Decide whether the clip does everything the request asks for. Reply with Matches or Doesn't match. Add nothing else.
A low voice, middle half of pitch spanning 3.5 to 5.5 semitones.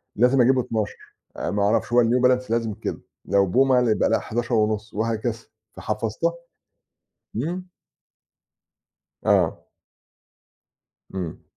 Doesn't match